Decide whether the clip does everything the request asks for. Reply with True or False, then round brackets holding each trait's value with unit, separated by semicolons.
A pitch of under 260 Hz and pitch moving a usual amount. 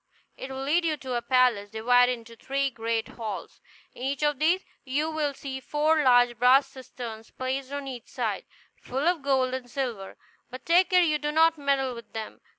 False (265 Hz; 3.3 semitones)